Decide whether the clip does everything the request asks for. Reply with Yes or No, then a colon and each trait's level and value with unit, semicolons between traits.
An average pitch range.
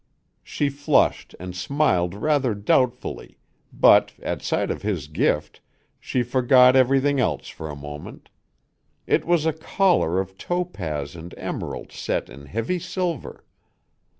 No: wide, 8.8 semitones